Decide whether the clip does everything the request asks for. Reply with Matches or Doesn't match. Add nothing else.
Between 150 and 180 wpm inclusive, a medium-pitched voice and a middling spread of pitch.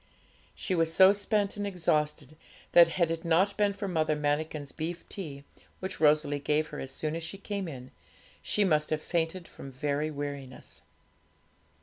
Matches